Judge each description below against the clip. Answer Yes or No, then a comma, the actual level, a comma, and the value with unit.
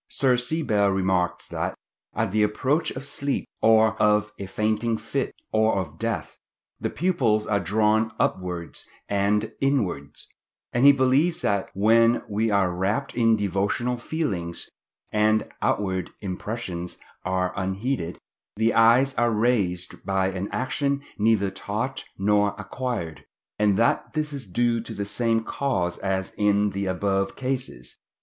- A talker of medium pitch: No, low, 105 Hz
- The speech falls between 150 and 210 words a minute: No, average, 140 wpm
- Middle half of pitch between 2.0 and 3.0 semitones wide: No, average, 3.9 semitones